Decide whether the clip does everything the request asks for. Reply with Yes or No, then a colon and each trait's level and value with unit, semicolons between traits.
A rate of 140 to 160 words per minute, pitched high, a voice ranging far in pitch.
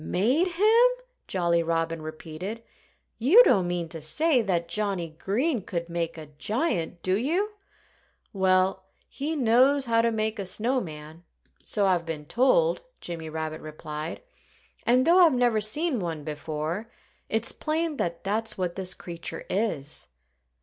Yes: average, 145 wpm; high, 195 Hz; wide, 7.2 semitones